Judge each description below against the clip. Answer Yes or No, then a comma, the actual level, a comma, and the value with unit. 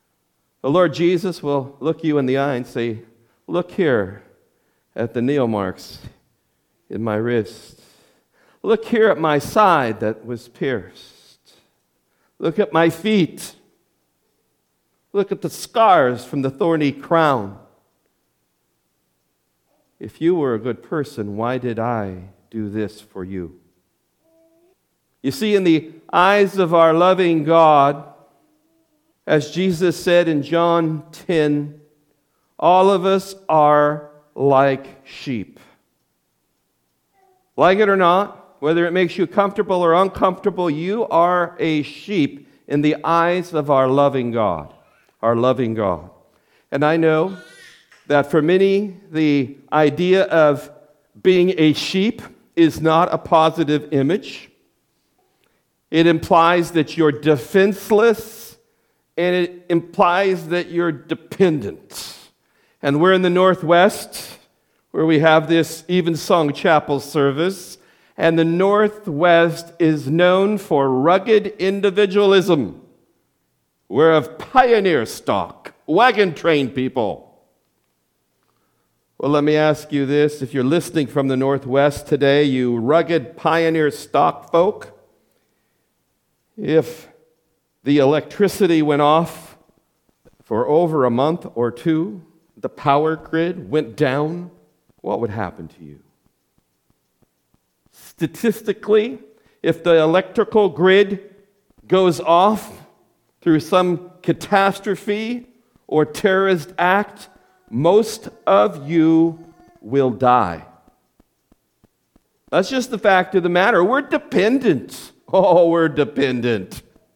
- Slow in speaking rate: Yes, slow, 115 wpm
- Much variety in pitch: No, average, 4.6 semitones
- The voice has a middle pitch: Yes, medium, 160 Hz